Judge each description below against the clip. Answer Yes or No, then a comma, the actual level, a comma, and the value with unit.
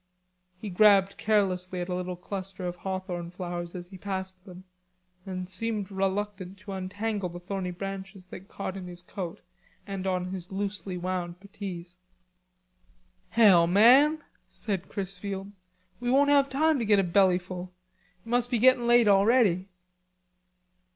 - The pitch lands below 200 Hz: Yes, high, 190 Hz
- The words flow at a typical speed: Yes, average, 145 wpm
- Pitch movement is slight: Yes, narrow, 2.3 semitones